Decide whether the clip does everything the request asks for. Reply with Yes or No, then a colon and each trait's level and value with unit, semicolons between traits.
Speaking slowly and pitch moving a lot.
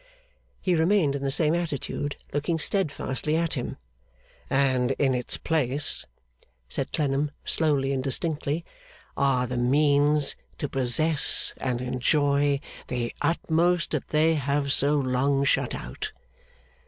No: slow, 125 wpm; average, 2.7 semitones